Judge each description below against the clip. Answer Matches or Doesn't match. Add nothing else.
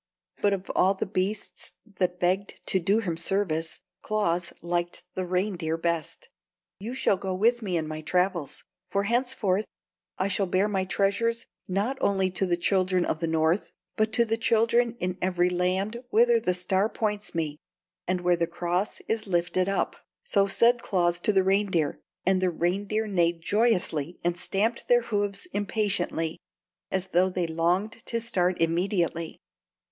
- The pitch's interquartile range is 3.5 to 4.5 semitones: Doesn't match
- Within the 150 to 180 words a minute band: Matches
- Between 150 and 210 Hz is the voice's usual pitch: Matches